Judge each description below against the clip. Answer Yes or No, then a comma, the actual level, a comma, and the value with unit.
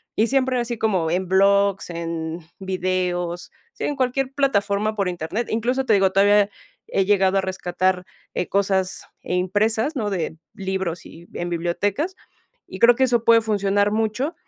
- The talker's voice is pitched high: Yes, high, 200 Hz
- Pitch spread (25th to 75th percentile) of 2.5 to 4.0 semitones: Yes, average, 3.4 semitones